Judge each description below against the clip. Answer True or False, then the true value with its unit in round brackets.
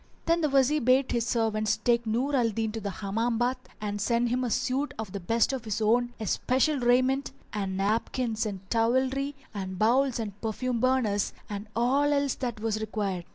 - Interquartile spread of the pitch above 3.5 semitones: False (3.2 semitones)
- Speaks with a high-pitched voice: True (235 Hz)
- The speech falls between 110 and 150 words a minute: False (190 wpm)